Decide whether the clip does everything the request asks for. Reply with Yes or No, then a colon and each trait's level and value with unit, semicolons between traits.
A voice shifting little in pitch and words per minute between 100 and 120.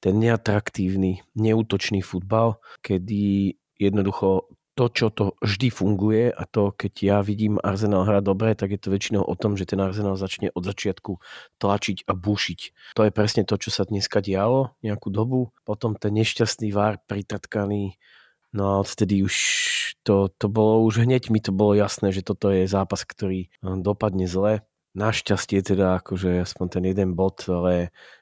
No: narrow, 1.9 semitones; fast, 165 wpm